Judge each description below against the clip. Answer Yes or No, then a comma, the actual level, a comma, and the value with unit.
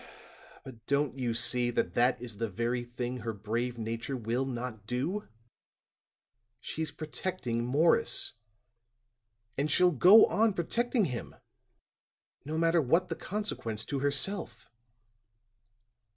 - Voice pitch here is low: Yes, low, 130 Hz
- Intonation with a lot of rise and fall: Yes, wide, 5.8 semitones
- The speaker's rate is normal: No, slow, 125 wpm